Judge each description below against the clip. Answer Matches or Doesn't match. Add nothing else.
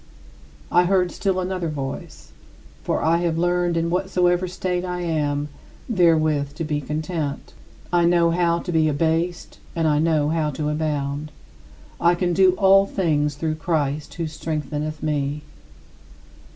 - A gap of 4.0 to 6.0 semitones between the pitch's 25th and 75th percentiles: Doesn't match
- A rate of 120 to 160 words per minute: Matches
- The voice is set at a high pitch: Doesn't match